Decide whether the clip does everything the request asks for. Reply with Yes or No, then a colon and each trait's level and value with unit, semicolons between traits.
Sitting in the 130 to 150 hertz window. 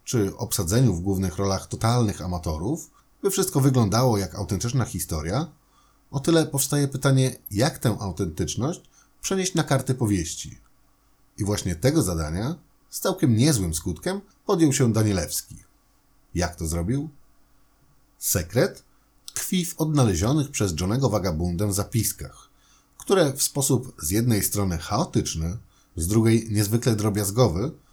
No: low, 115 Hz